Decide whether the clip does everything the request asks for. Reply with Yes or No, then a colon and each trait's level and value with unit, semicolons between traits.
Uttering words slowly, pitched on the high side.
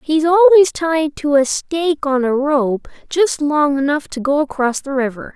No: average, 190 wpm; very high, 295 Hz